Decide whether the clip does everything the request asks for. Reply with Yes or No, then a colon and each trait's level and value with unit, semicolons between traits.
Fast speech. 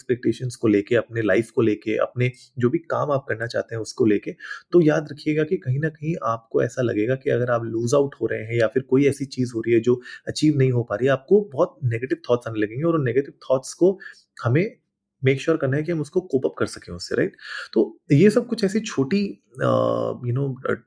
Yes: fast, 245 wpm